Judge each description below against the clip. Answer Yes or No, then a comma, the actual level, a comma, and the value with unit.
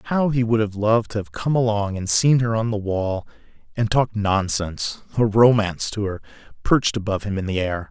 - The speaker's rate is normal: No, fast, 210 wpm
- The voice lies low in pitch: Yes, low, 105 Hz